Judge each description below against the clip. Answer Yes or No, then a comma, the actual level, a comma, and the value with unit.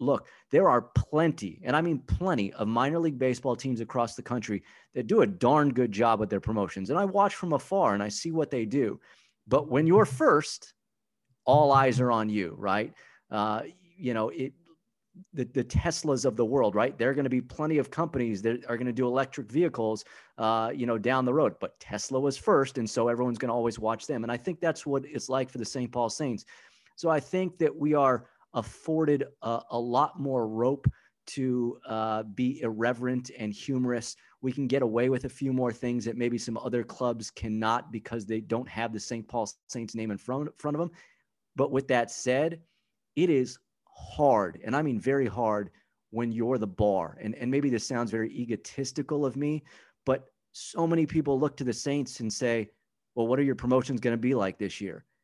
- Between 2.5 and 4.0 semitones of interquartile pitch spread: Yes, average, 3.3 semitones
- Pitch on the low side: Yes, low, 125 Hz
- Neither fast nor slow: No, fast, 215 wpm